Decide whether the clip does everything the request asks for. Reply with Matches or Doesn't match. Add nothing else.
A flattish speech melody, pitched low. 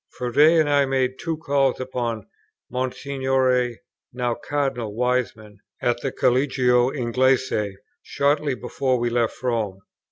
Matches